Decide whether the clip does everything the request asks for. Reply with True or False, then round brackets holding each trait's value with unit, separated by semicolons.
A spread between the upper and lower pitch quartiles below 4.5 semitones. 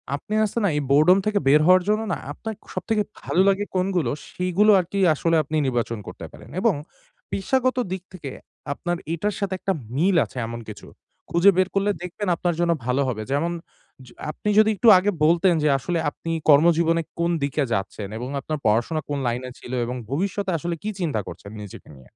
False (5.6 semitones)